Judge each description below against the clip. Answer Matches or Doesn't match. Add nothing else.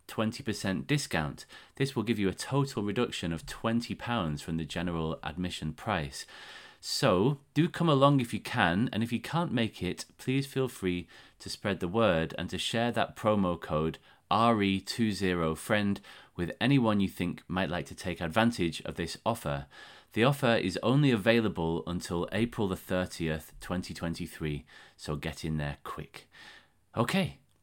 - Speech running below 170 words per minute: Matches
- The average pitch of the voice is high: Doesn't match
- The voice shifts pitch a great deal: Matches